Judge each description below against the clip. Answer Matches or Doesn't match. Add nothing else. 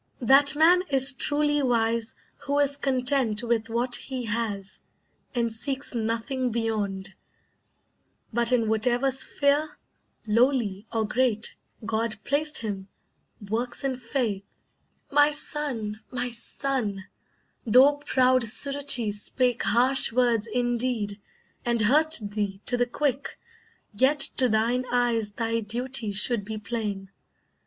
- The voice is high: Matches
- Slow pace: Matches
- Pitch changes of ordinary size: Matches